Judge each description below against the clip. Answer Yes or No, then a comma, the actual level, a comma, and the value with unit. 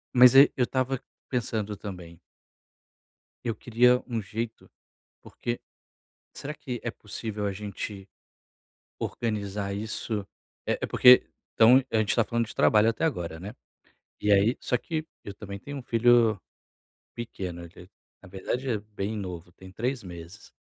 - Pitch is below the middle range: Yes, low, 110 Hz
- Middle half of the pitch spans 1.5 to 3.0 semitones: No, average, 3.5 semitones